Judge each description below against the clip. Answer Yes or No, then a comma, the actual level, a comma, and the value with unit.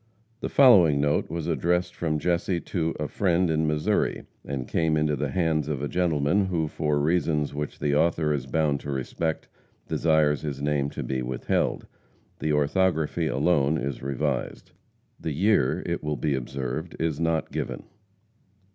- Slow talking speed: No, average, 160 wpm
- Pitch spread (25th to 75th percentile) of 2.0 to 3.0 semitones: Yes, narrow, 2.6 semitones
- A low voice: Yes, very low, 75 Hz